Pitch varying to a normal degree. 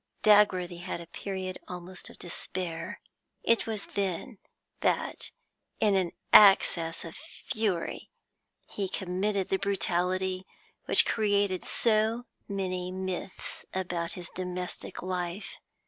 No: narrow, 2.0 semitones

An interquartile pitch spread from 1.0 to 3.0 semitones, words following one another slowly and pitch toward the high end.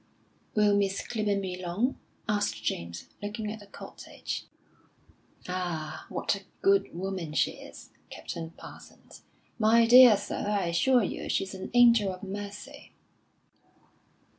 Yes: narrow, 2.6 semitones; slow, 130 wpm; high, 200 Hz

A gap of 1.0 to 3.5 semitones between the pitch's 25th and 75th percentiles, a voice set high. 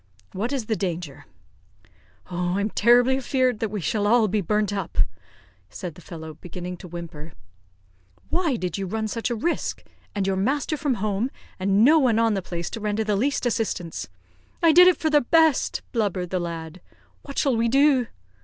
No: wide, 5.6 semitones; high, 215 Hz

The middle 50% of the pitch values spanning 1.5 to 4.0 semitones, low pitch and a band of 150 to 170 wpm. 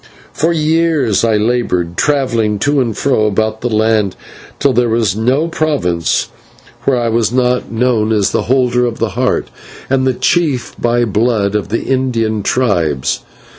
Yes: average, 3.3 semitones; low, 120 Hz; average, 160 wpm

